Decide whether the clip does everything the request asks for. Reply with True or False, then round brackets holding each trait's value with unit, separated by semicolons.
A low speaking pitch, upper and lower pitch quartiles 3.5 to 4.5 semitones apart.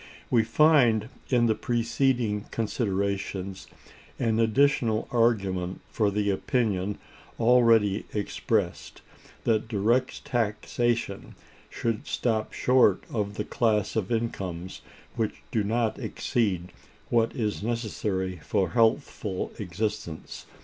False (110 Hz; 2.8 semitones)